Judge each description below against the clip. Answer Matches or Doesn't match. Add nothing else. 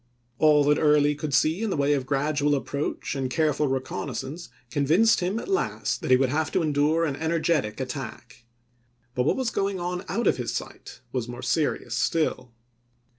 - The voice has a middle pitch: Matches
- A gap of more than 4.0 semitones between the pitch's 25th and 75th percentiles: Doesn't match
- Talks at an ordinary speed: Matches